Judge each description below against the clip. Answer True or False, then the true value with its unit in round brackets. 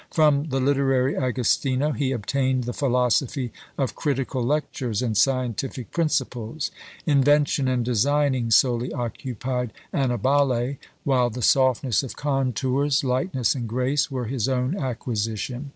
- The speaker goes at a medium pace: False (120 wpm)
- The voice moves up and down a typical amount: False (2.2 semitones)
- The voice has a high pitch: False (130 Hz)